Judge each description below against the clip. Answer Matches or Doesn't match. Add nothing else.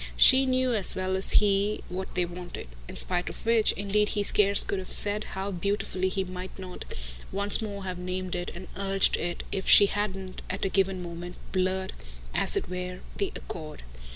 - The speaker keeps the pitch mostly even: Matches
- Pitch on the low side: Doesn't match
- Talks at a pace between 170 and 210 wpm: Matches